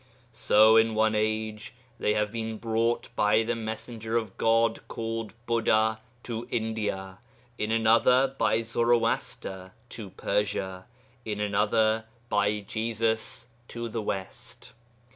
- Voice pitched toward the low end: Yes, low, 110 Hz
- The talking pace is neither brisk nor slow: No, slow, 120 wpm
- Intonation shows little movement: Yes, narrow, 1.4 semitones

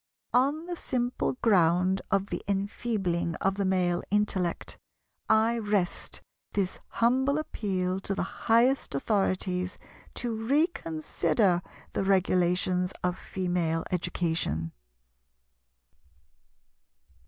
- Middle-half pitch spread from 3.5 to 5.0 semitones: Yes, average, 3.9 semitones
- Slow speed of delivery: Yes, slow, 95 wpm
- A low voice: No, high, 190 Hz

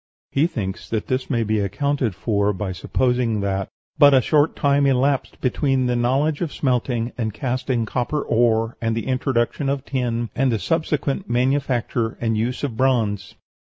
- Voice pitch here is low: Yes, low, 125 Hz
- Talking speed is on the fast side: No, average, 165 wpm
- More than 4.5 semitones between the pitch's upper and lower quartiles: No, average, 3.3 semitones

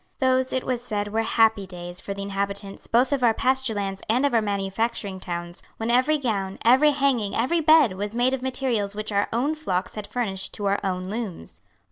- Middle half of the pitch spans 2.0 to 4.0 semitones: No, average, 4.6 semitones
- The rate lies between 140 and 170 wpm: No, fast, 205 wpm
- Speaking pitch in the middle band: No, high, 220 Hz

